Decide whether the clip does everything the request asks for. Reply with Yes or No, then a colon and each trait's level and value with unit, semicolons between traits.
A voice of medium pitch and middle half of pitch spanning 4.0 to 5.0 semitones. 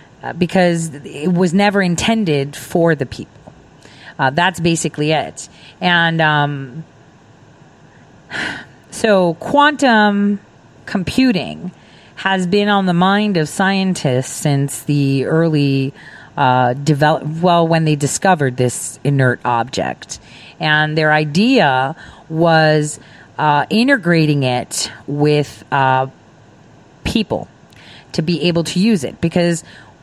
Yes: medium, 160 Hz; average, 4.5 semitones